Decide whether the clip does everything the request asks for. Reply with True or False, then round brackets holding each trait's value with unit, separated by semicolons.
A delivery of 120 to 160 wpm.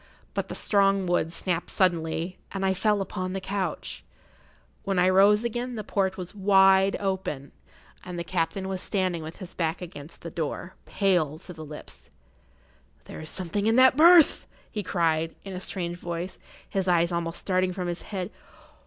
False (175 wpm)